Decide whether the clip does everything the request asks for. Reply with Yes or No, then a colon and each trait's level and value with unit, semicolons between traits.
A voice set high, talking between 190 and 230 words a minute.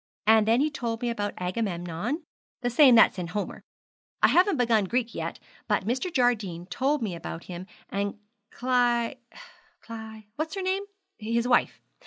No: high, 230 Hz; average, 160 wpm